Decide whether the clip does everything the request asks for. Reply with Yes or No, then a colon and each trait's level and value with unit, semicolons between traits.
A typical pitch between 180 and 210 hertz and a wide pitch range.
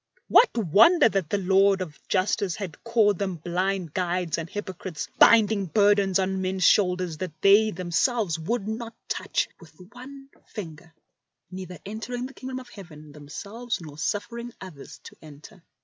No: high, 190 Hz; average, 4.1 semitones